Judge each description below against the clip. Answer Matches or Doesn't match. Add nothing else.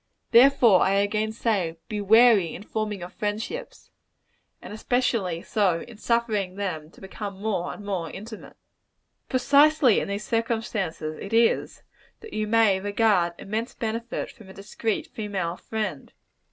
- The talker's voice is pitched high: Matches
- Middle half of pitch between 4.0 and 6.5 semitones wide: Doesn't match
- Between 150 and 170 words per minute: Doesn't match